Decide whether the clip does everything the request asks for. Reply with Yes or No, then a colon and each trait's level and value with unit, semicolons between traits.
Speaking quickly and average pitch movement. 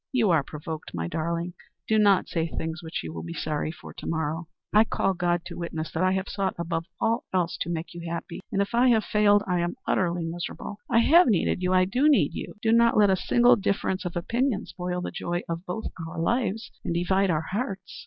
Yes: fast, 230 wpm; average, 3.8 semitones